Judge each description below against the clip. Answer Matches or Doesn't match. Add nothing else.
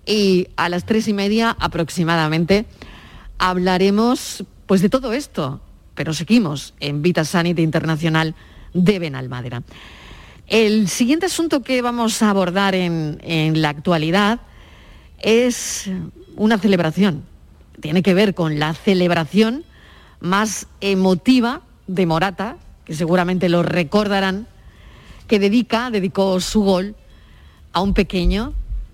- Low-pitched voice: Doesn't match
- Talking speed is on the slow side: Matches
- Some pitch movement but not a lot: Matches